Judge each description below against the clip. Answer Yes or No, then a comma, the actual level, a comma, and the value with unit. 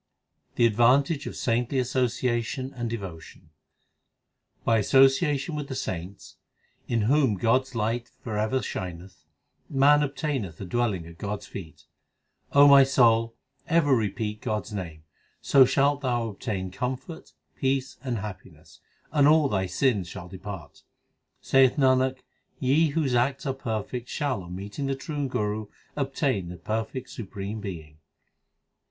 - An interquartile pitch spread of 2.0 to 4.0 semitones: No, average, 5.0 semitones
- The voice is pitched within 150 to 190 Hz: No, low, 120 Hz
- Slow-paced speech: No, average, 145 wpm